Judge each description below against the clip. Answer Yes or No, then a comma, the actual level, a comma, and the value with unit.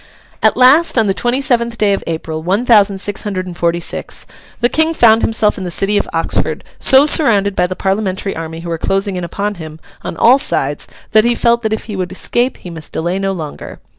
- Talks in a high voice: Yes, high, 200 Hz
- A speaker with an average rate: No, fast, 225 wpm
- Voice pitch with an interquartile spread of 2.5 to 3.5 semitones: No, average, 4.7 semitones